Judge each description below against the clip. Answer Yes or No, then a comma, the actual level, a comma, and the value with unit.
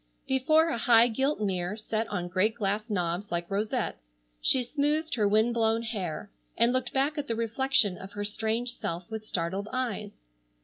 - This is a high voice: Yes, high, 220 Hz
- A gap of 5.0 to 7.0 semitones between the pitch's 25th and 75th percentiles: No, average, 3.7 semitones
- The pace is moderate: Yes, average, 175 wpm